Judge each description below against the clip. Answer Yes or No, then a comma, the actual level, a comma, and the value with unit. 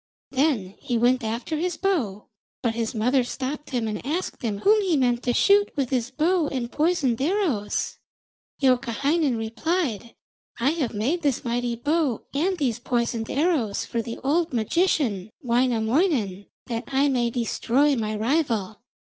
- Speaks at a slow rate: No, average, 150 wpm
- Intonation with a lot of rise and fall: No, average, 4.9 semitones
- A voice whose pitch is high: Yes, very high, 255 Hz